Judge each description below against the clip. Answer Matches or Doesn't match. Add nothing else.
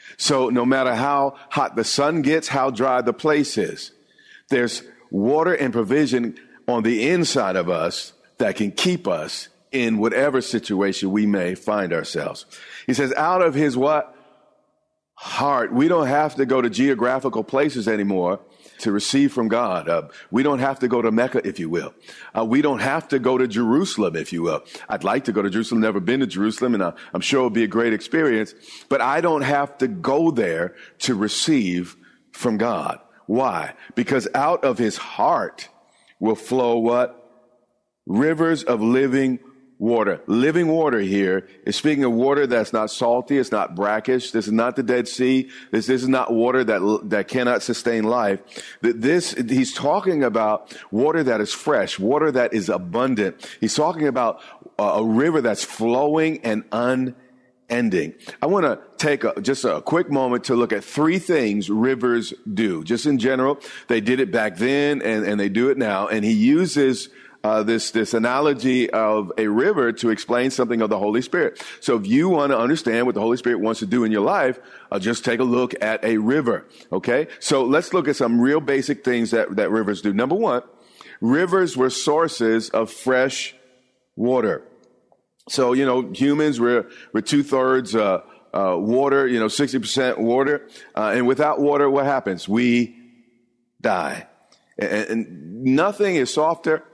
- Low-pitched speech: Matches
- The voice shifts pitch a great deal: Doesn't match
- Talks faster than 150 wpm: Matches